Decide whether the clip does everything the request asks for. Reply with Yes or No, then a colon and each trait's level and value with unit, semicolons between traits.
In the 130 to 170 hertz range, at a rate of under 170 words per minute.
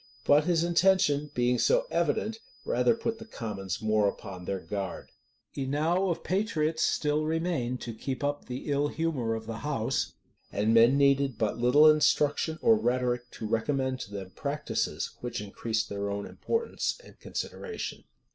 Yes: low, 135 Hz; average, 155 wpm